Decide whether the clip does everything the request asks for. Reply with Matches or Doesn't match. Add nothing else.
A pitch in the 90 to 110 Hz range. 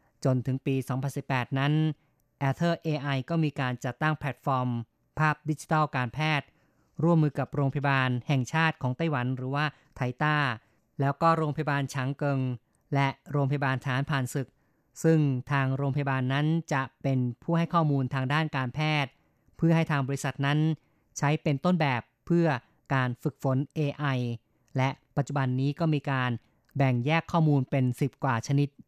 Doesn't match